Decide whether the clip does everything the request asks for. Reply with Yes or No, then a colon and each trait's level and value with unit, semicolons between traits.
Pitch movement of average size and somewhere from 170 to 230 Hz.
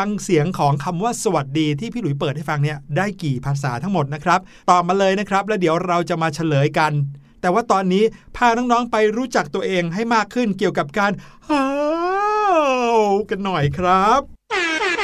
No: wide, 6.4 semitones; high, 190 Hz